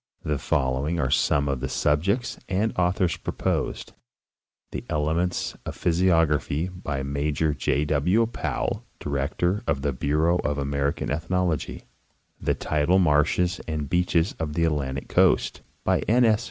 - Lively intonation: No, average, 3.8 semitones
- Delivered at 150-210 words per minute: No, average, 140 wpm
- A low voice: Yes, very low, 80 Hz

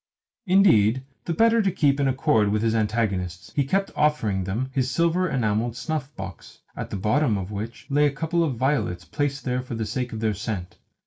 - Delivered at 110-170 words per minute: No, average, 200 wpm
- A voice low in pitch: Yes, low, 125 Hz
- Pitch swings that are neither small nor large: No, wide, 5.8 semitones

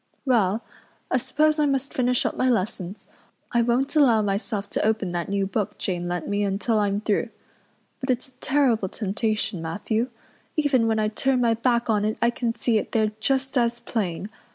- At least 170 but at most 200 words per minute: Yes, average, 190 wpm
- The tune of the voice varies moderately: Yes, average, 3.6 semitones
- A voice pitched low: No, high, 225 Hz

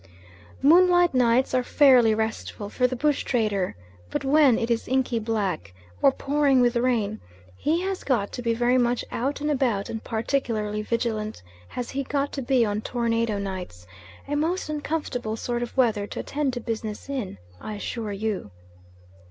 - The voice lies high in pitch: Yes, high, 240 Hz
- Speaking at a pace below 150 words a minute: No, average, 170 wpm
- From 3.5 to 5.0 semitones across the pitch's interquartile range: Yes, average, 4.0 semitones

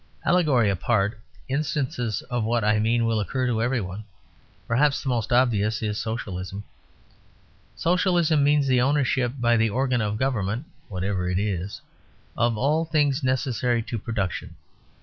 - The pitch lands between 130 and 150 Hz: No, low, 120 Hz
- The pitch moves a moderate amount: Yes, average, 4.0 semitones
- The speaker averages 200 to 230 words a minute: No, average, 145 wpm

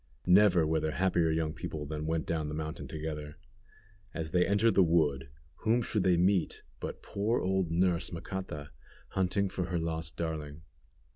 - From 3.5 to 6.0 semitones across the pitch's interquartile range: No, average, 3.0 semitones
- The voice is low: Yes, very low, 85 Hz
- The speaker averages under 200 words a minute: Yes, average, 165 wpm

